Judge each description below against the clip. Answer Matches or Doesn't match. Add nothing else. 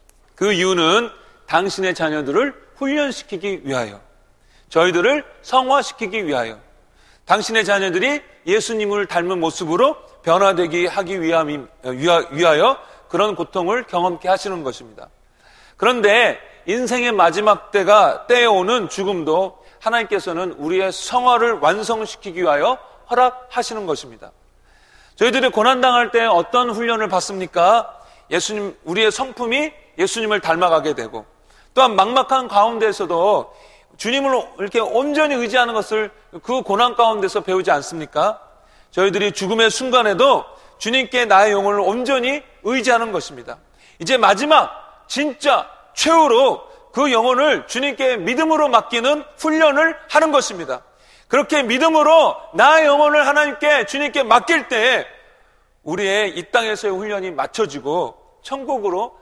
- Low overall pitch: Doesn't match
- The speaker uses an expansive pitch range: Matches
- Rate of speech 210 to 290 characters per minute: Doesn't match